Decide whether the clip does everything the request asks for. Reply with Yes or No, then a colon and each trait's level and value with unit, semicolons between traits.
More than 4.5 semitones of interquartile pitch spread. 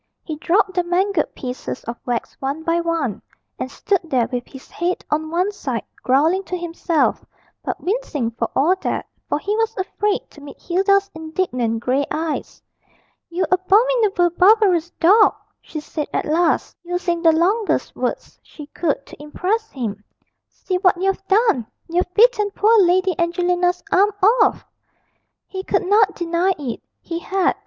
No: average, 4.1 semitones